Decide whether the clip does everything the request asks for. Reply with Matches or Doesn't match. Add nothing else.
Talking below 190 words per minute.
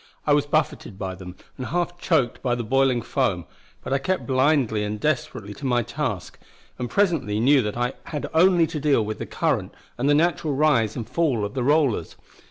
Doesn't match